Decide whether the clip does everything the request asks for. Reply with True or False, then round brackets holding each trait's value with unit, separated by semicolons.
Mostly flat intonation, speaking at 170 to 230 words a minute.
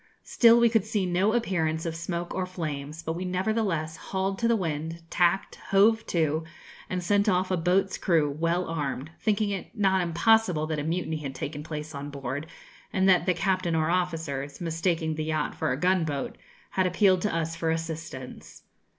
False (3.2 semitones; 185 wpm)